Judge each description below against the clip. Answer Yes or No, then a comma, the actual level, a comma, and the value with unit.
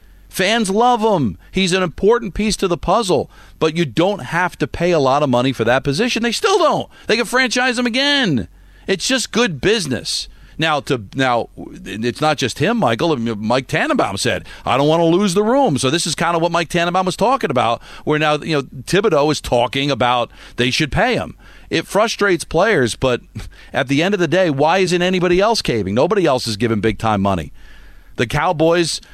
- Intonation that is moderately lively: No, wide, 7.4 semitones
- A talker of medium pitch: Yes, medium, 165 Hz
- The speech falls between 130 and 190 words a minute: No, fast, 205 wpm